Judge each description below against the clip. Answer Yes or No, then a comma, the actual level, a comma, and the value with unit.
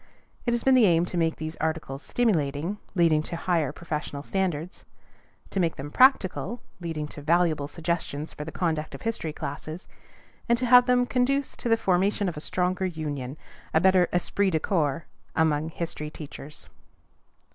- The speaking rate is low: No, average, 170 wpm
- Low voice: No, medium, 170 Hz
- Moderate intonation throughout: Yes, average, 3.9 semitones